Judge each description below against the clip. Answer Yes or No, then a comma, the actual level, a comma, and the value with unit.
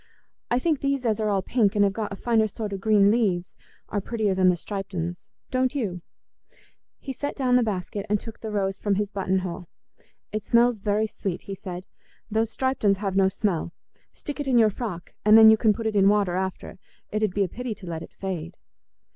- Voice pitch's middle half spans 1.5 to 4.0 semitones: Yes, average, 2.9 semitones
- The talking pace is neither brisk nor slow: No, fast, 225 wpm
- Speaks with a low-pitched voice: No, high, 205 Hz